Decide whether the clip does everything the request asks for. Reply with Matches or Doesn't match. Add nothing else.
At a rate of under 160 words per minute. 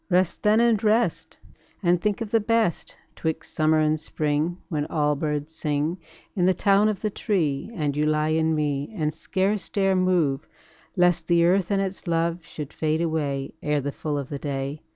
Doesn't match